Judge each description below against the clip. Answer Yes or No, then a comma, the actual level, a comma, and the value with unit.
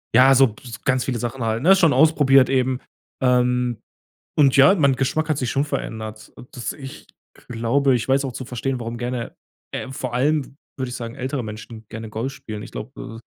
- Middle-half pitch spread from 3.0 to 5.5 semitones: No, narrow, 2.6 semitones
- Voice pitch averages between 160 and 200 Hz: No, low, 125 Hz